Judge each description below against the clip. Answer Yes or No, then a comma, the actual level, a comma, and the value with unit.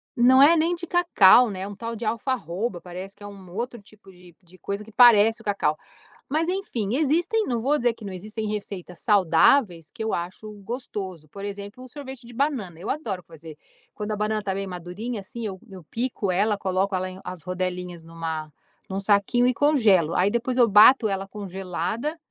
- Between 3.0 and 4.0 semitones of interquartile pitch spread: No, average, 4.6 semitones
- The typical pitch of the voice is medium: No, high, 205 Hz